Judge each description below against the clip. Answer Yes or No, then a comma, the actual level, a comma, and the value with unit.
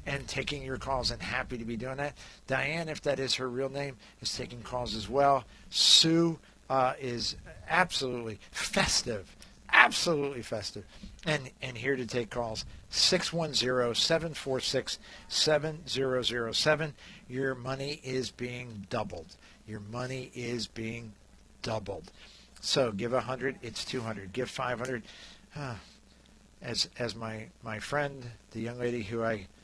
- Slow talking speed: Yes, slow, 130 wpm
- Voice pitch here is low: Yes, low, 125 Hz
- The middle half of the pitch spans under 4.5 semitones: Yes, average, 3.1 semitones